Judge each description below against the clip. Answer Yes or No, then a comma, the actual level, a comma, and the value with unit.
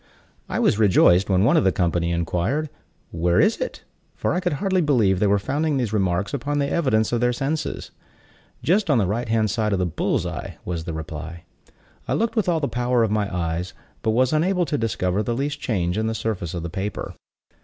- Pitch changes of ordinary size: No, wide, 7.6 semitones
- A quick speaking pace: Yes, fast, 220 wpm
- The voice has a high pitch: No, low, 110 Hz